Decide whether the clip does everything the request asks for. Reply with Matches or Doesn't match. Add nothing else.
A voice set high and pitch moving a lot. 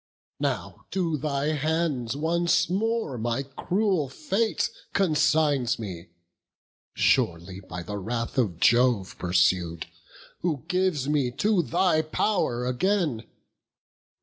Doesn't match